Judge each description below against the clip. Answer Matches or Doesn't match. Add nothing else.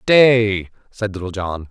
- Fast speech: Doesn't match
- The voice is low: Matches